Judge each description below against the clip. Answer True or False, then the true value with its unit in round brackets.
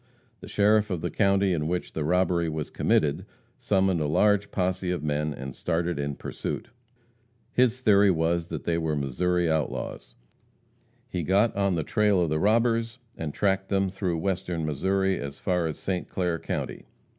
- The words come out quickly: False (170 wpm)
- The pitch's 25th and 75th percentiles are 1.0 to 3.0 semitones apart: False (3.7 semitones)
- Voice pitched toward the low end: True (90 Hz)